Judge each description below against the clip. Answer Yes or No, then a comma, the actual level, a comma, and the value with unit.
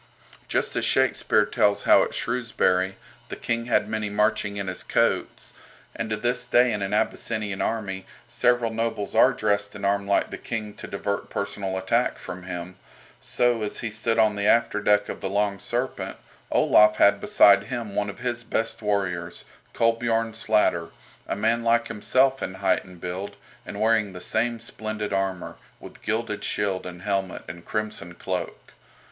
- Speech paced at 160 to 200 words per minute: Yes, average, 170 wpm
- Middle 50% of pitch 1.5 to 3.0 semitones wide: Yes, average, 2.7 semitones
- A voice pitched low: Yes, low, 105 Hz